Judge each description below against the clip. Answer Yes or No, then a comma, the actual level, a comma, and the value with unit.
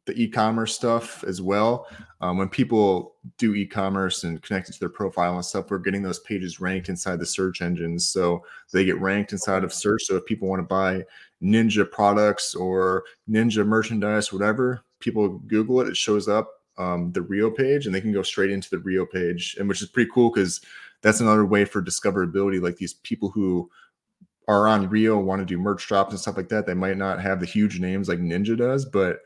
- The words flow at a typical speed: No, fast, 210 wpm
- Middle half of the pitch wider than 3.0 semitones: No, narrow, 2.6 semitones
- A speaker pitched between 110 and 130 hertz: No, low, 100 Hz